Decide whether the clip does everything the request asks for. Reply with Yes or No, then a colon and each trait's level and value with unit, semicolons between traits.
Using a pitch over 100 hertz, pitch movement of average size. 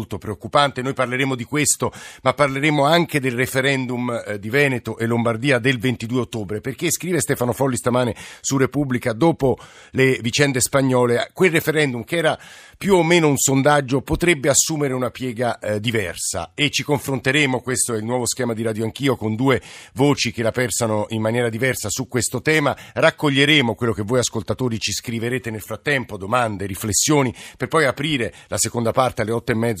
Yes: low, 125 Hz; average, 3.6 semitones